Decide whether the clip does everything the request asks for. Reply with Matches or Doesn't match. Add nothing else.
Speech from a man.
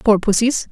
Doesn't match